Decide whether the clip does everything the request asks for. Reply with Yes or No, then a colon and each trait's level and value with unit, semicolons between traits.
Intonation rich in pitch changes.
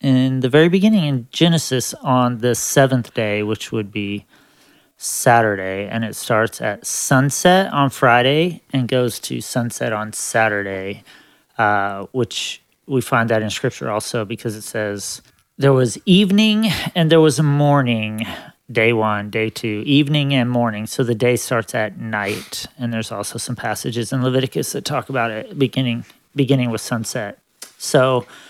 No: average, 3.8 semitones